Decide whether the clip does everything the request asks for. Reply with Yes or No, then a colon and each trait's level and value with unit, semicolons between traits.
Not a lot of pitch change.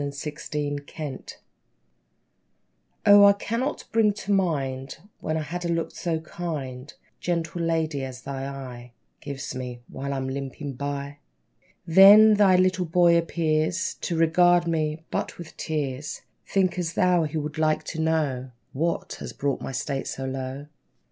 No: average, 4.0 semitones